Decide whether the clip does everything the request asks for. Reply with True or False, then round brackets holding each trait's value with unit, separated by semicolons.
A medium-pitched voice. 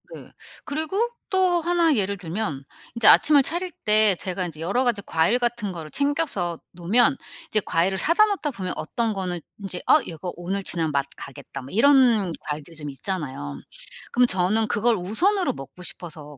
False (200 Hz)